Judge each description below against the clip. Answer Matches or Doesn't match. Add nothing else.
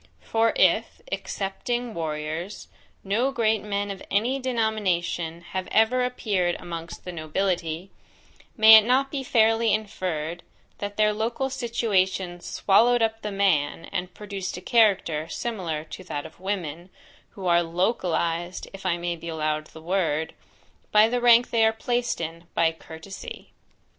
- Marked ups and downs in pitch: Doesn't match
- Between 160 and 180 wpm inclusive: Doesn't match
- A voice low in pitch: Doesn't match